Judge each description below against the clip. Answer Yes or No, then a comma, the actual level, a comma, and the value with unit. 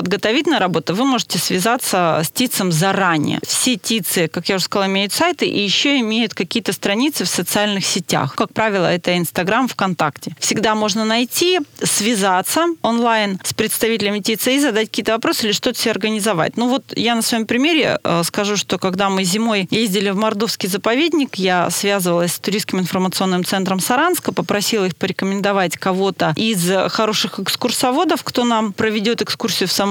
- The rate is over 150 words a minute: Yes, fast, 160 wpm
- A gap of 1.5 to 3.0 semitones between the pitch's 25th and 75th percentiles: No, average, 3.4 semitones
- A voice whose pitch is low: No, high, 210 Hz